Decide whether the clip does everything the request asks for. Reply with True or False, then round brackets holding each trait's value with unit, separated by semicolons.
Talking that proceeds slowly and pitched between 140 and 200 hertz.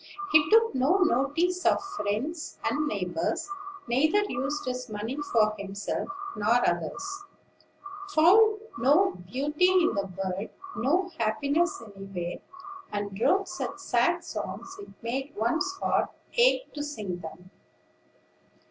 False (120 wpm; 275 Hz)